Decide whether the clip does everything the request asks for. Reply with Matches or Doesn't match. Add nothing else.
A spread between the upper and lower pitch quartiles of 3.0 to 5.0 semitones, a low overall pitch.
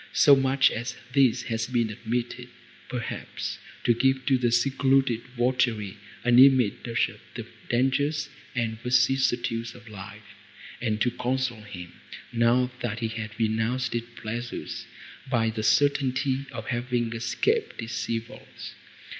Doesn't match